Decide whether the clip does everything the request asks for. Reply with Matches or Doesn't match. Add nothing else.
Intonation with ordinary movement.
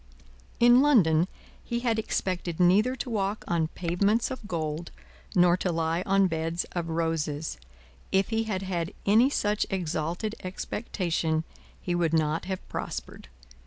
Matches